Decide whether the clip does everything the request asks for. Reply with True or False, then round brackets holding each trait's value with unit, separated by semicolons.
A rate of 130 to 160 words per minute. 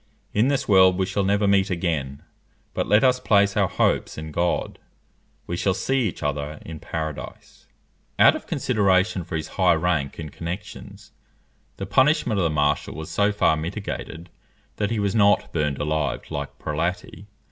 False (170 wpm)